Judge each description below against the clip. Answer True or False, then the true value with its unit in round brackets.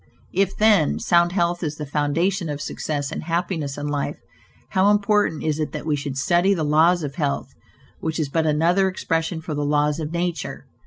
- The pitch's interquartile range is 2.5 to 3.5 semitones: True (3.0 semitones)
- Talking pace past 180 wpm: True (195 wpm)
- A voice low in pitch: False (160 Hz)